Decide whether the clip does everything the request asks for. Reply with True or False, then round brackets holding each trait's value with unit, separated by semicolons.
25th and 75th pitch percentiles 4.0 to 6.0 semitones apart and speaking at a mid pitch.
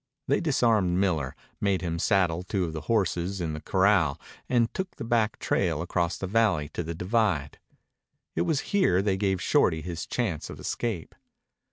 False (4.5 semitones; 95 Hz)